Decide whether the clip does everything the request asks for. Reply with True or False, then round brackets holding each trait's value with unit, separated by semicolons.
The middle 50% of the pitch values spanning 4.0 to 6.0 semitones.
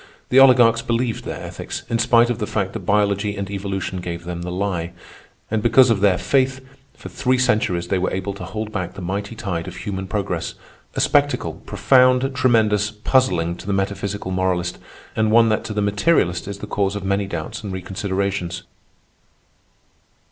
False (3.4 semitones)